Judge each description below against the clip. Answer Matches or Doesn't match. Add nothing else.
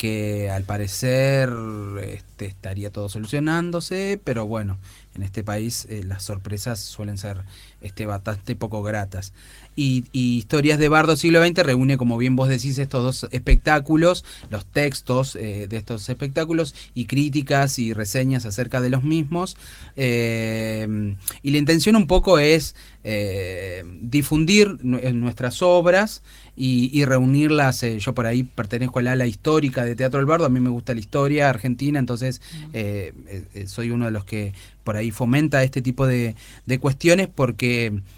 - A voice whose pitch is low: Matches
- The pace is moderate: Matches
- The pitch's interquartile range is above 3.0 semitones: Matches